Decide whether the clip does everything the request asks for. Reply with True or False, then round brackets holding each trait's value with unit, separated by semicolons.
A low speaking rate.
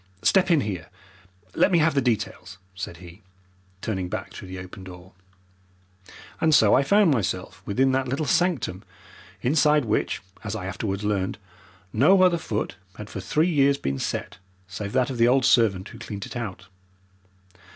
False (170 wpm)